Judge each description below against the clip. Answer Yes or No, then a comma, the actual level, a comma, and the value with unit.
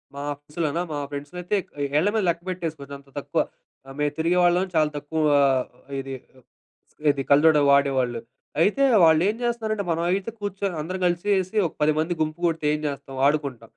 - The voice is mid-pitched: Yes, medium, 160 Hz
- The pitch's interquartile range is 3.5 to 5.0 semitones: Yes, average, 4.3 semitones